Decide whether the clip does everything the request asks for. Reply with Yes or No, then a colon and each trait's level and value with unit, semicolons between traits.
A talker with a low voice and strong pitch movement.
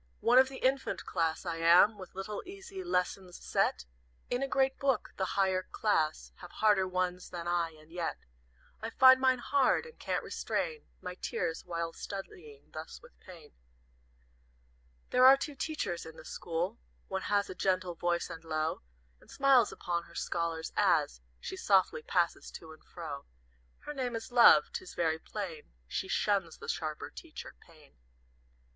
No: medium, 185 Hz; wide, 6.8 semitones